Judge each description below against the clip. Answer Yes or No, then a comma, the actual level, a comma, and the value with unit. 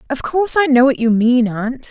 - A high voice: Yes, very high, 260 Hz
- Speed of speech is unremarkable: No, fast, 250 wpm